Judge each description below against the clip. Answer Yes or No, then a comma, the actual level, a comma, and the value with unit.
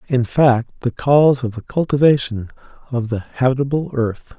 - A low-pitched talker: Yes, low, 125 Hz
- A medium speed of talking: Yes, average, 150 wpm